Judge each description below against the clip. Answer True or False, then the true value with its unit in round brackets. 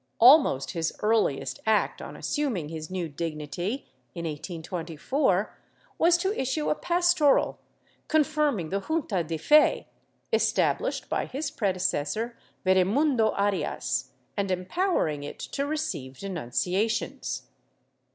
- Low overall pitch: False (200 Hz)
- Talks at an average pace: False (110 wpm)